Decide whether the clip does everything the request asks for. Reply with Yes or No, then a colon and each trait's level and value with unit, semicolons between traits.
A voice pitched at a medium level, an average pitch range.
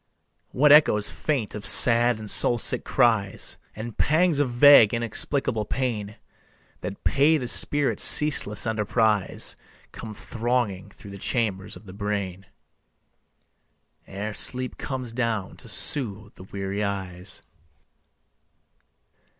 No: low, 110 Hz; average, 3.9 semitones